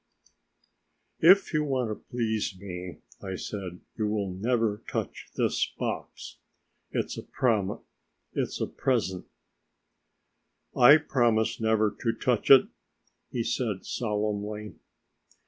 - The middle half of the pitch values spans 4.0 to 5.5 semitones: No, average, 3.1 semitones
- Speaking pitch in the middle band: No, low, 110 Hz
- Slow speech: Yes, slow, 100 wpm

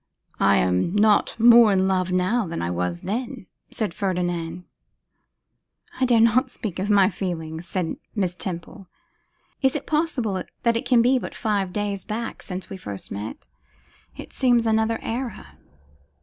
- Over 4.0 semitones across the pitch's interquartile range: Yes, average, 4.5 semitones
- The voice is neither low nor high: No, high, 200 Hz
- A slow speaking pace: No, average, 155 wpm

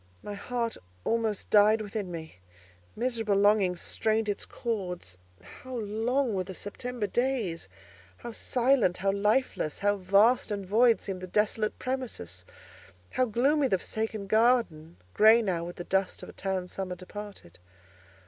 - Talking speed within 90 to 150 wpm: Yes, average, 140 wpm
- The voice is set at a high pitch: Yes, high, 210 Hz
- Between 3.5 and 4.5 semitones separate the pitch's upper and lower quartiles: Yes, average, 3.9 semitones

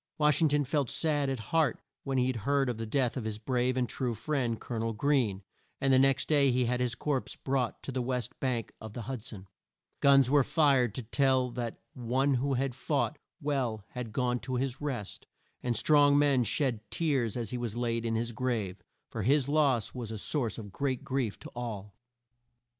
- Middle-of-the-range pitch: No, low, 125 Hz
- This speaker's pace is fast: Yes, fast, 210 wpm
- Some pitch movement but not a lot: Yes, average, 3.0 semitones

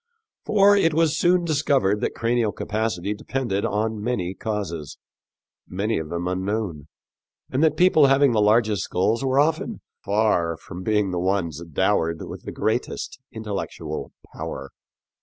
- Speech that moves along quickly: No, average, 140 wpm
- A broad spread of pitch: Yes, wide, 6.3 semitones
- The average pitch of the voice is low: Yes, low, 105 Hz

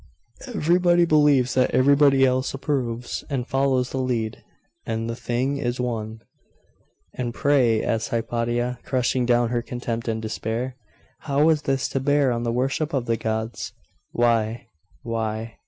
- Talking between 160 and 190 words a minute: No, average, 145 wpm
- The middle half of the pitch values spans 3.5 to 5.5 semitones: No, average, 2.7 semitones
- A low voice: Yes, low, 125 Hz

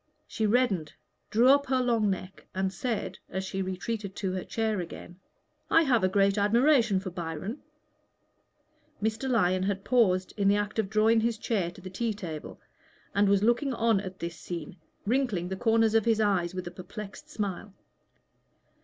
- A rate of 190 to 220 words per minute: No, average, 175 wpm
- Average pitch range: Yes, average, 3.3 semitones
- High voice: Yes, high, 205 Hz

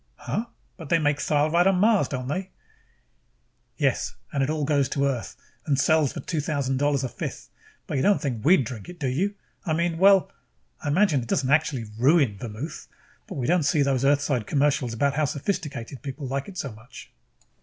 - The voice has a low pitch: No, medium, 145 Hz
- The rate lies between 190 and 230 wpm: Yes, average, 195 wpm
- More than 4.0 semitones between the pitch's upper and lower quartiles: No, average, 3.6 semitones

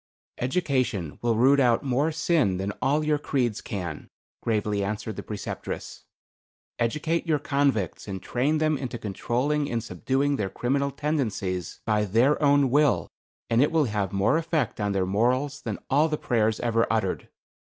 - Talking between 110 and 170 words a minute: Yes, average, 160 wpm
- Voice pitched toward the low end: Yes, low, 125 Hz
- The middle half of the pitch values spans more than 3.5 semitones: Yes, wide, 5.4 semitones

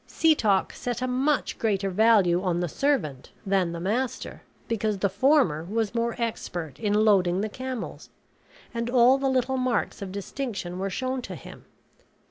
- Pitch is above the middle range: Yes, high, 220 Hz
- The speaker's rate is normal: Yes, average, 160 wpm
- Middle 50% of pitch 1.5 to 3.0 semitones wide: No, average, 5.1 semitones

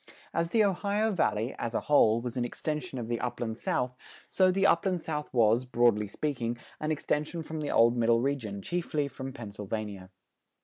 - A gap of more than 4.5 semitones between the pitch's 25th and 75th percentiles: Yes, wide, 5.4 semitones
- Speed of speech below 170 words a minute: No, average, 175 wpm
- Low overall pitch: Yes, low, 130 Hz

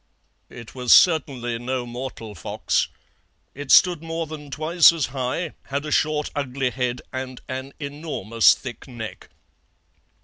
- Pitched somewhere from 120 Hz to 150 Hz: Yes, low, 135 Hz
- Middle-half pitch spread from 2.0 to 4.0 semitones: Yes, average, 3.6 semitones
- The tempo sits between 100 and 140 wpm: Yes, slow, 135 wpm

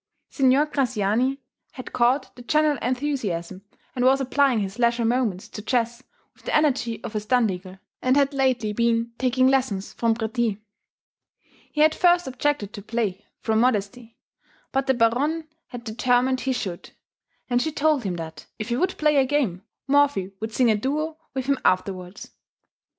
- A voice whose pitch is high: Yes, high, 245 Hz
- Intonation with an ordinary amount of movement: Yes, average, 3.9 semitones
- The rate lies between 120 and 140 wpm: No, average, 165 wpm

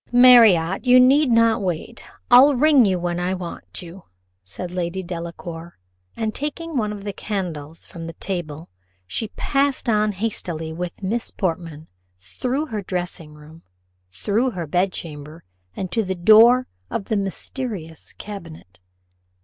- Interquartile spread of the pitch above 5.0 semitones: Yes, wide, 5.4 semitones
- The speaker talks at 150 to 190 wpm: No, average, 140 wpm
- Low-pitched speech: No, high, 190 Hz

